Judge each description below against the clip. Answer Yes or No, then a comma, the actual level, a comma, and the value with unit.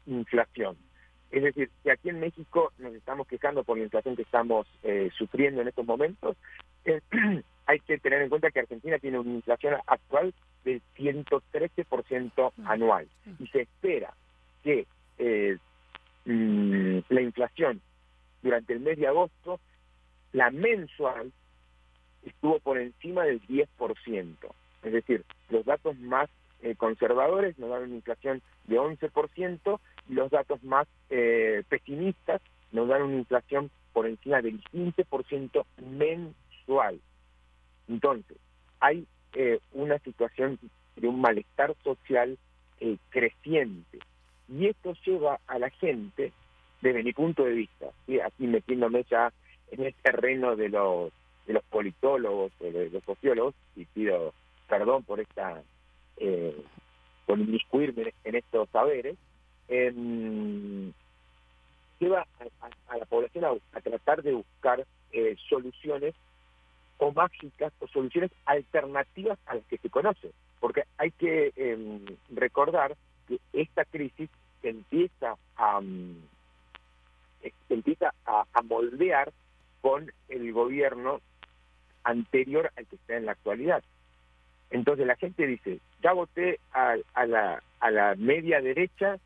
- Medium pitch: No, low, 125 Hz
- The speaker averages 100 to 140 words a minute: Yes, average, 130 wpm